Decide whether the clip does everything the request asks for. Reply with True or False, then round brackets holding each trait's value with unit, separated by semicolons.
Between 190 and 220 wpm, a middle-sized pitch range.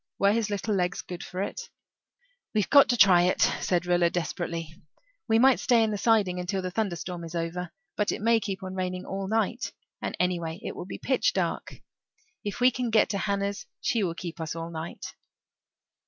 True (200 wpm; 3.6 semitones)